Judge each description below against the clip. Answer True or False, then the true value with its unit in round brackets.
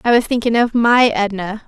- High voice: True (225 Hz)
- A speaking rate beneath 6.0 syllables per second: True (5.3 syllables/s)